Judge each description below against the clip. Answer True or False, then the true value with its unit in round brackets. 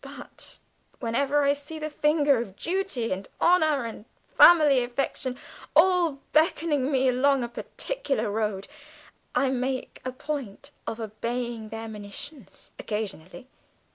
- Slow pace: True (125 wpm)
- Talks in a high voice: True (260 Hz)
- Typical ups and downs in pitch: True (4.7 semitones)